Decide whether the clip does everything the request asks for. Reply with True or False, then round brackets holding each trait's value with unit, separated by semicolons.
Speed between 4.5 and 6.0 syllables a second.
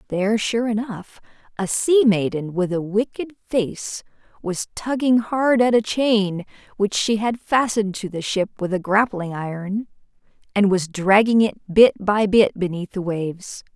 False (4.3 syllables/s)